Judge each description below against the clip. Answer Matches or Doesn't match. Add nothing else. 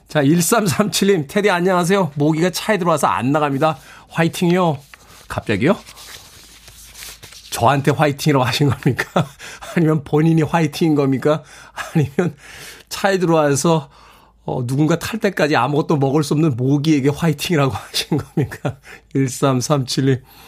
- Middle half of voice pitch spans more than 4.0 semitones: Doesn't match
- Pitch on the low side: Doesn't match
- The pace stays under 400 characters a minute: Matches